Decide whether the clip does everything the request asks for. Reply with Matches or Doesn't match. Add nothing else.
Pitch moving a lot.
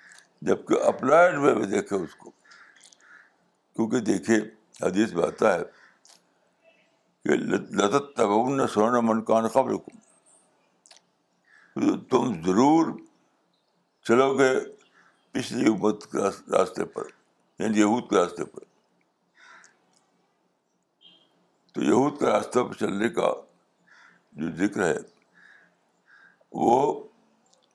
Doesn't match